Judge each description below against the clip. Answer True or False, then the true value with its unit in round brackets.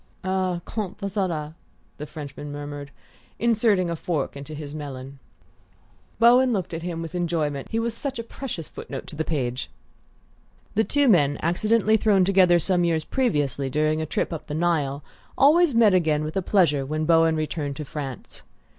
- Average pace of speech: True (175 wpm)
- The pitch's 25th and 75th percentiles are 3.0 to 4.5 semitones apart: False (5.1 semitones)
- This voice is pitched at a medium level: True (165 Hz)